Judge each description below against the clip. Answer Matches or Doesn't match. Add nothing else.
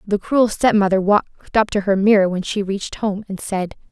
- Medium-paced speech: Doesn't match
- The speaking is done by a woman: Matches